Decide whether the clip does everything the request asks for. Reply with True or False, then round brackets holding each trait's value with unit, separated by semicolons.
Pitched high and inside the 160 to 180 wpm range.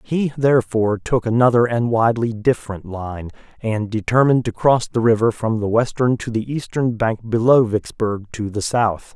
False (115 Hz; 170 wpm)